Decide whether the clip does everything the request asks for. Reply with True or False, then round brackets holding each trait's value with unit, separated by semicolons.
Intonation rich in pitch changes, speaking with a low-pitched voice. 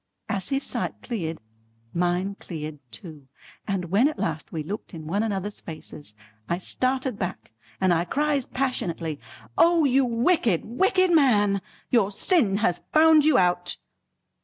False (7.3 semitones; 200 Hz)